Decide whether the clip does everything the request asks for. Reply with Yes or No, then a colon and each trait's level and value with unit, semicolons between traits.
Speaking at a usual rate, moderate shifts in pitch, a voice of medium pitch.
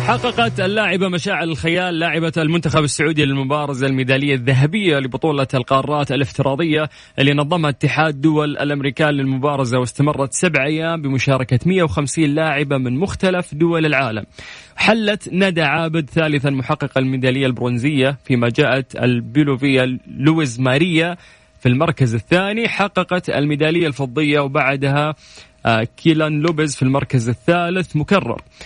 Yes: average, 115 wpm; average, 3.5 semitones; medium, 150 Hz